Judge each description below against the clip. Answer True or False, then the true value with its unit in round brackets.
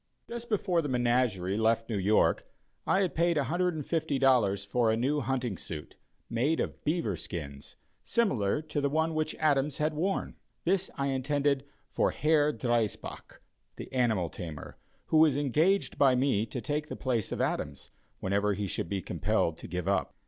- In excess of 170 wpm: False (165 wpm)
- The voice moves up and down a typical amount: False (6.8 semitones)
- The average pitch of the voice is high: False (130 Hz)